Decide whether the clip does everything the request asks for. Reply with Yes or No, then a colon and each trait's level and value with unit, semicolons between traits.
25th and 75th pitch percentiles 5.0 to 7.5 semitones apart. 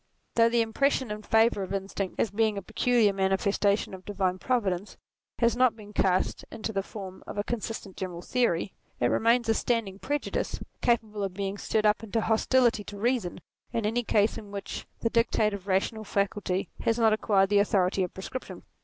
No: average, 2.9 semitones